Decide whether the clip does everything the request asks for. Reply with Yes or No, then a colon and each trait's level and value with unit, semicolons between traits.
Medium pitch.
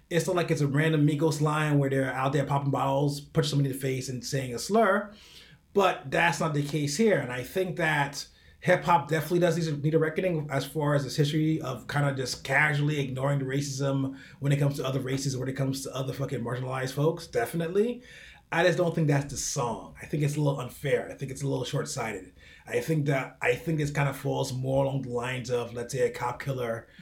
Yes: medium, 145 Hz